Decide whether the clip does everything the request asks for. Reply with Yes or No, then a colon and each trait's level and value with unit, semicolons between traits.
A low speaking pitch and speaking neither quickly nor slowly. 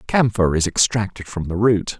Yes: low, 100 Hz; average, 180 wpm